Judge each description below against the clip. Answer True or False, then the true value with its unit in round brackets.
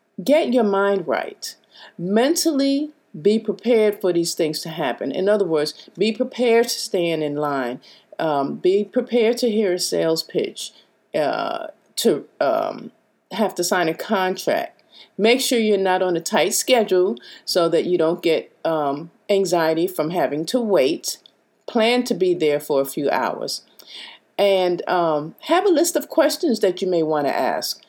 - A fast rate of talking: False (165 wpm)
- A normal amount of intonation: False (6.3 semitones)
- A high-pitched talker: True (200 Hz)